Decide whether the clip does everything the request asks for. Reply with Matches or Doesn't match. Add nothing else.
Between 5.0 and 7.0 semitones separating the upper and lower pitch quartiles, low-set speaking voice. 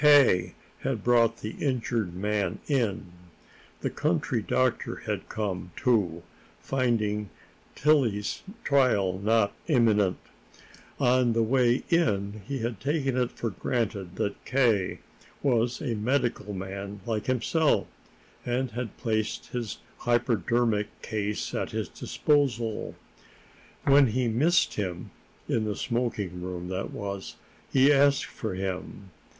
Doesn't match